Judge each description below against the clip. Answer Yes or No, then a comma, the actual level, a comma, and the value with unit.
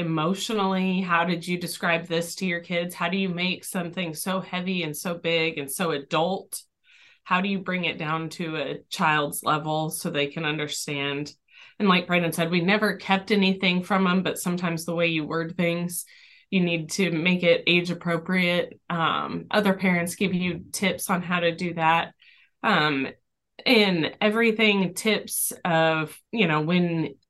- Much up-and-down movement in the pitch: No, average, 2.7 semitones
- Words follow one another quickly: No, average, 175 wpm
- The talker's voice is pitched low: No, medium, 175 Hz